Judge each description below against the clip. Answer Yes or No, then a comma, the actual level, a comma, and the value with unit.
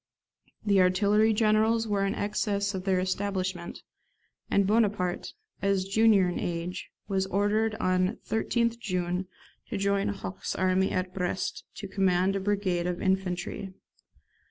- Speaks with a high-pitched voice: Yes, high, 195 Hz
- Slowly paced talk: Yes, slow, 130 wpm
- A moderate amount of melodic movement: No, narrow, 2.0 semitones